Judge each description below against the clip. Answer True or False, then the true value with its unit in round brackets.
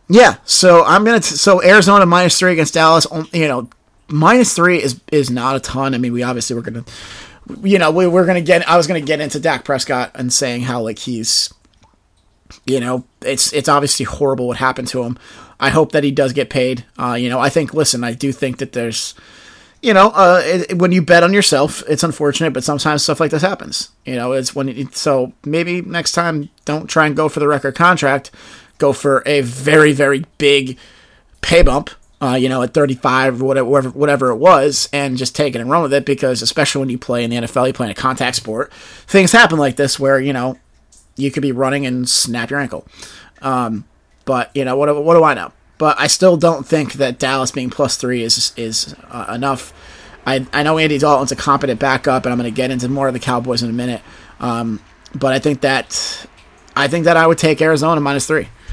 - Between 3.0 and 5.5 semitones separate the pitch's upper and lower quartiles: True (3.8 semitones)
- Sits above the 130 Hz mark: True (140 Hz)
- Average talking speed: False (220 wpm)